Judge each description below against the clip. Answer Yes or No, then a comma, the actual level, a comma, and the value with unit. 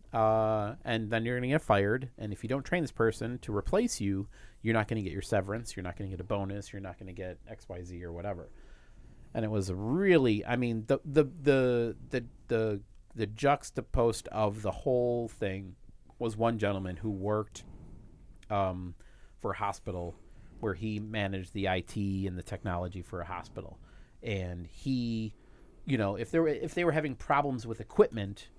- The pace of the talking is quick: No, average, 190 wpm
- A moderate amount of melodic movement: Yes, average, 3.4 semitones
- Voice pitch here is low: Yes, low, 105 Hz